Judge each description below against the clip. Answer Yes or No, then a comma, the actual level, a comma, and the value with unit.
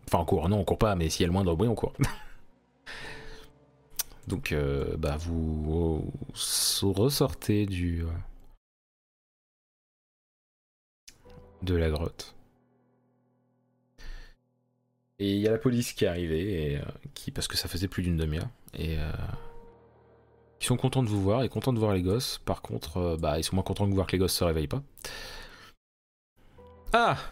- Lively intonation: Yes, wide, 6.8 semitones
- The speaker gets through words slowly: No, average, 175 wpm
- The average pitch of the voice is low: Yes, low, 100 Hz